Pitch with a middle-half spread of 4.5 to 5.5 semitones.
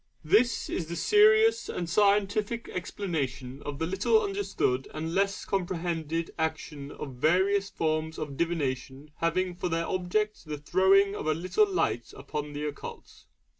Yes: average, 4.8 semitones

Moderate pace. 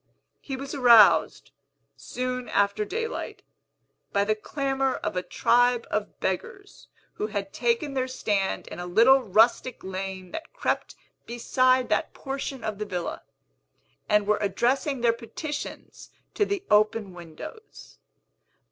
No: slow, 130 wpm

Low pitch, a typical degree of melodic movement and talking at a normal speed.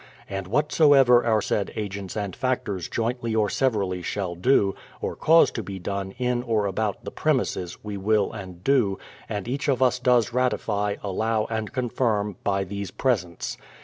Yes: low, 105 Hz; average, 4.0 semitones; average, 165 wpm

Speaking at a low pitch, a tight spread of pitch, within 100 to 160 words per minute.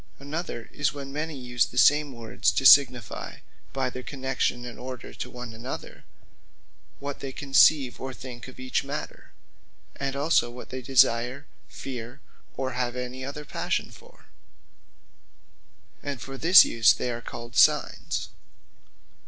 Yes: low, 130 Hz; narrow, 2.2 semitones; average, 145 wpm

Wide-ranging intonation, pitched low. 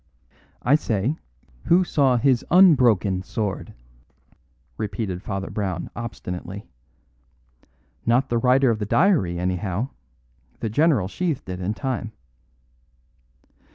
Yes: wide, 5.8 semitones; low, 115 Hz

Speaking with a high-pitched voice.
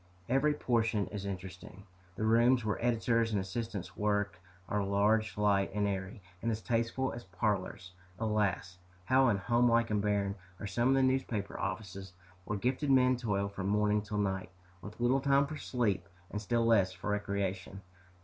No: low, 105 Hz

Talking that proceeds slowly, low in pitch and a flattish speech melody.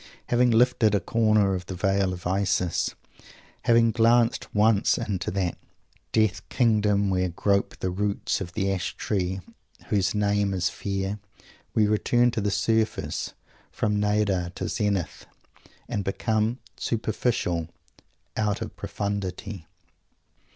Yes: slow, 125 wpm; low, 100 Hz; narrow, 2.3 semitones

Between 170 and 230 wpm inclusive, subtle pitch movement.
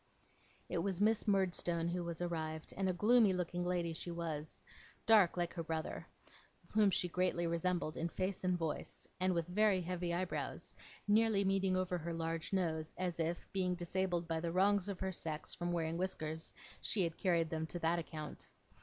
Yes: average, 180 wpm; narrow, 2.1 semitones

